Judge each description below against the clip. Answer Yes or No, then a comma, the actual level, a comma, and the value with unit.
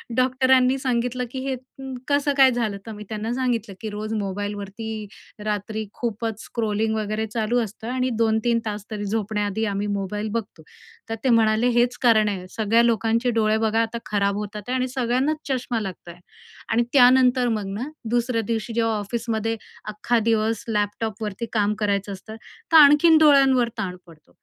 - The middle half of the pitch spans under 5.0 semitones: Yes, average, 2.8 semitones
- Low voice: No, high, 225 Hz